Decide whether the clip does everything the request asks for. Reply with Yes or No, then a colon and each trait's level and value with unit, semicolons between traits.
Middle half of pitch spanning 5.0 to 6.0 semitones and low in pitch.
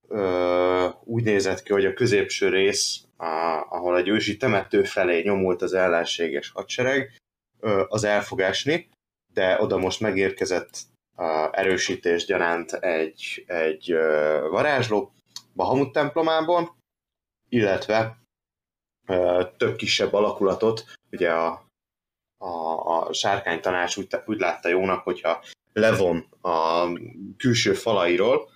Yes: wide, 5.6 semitones; very low, 95 Hz